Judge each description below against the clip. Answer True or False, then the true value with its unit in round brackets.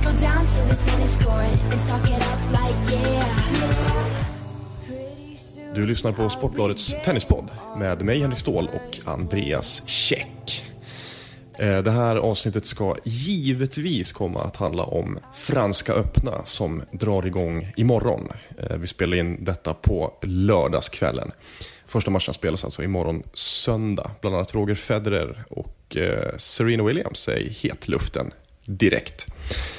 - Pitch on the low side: True (110 Hz)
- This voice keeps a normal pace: False (105 wpm)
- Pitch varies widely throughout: False (4.0 semitones)